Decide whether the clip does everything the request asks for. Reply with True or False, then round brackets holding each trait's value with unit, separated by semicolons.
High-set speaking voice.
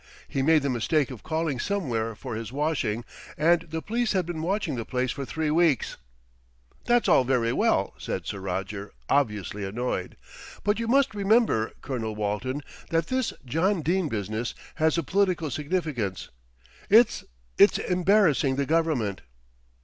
False (150 Hz)